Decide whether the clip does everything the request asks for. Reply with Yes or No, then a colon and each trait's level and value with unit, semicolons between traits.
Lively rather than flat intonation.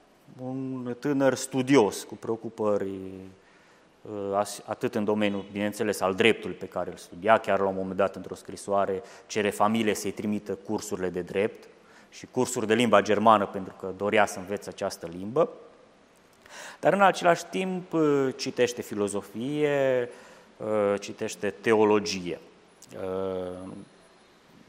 No: average, 4.2 semitones